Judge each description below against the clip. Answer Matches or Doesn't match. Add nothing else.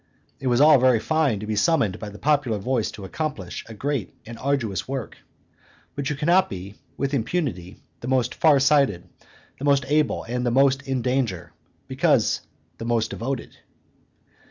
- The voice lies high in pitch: Doesn't match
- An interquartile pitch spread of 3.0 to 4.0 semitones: Doesn't match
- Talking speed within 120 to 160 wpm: Doesn't match